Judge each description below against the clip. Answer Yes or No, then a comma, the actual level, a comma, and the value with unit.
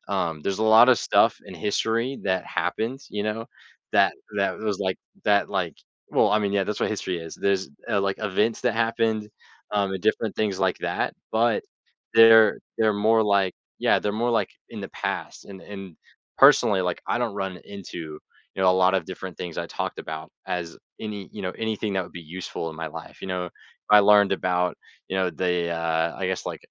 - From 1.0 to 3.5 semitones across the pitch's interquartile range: Yes, average, 2.9 semitones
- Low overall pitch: Yes, low, 100 Hz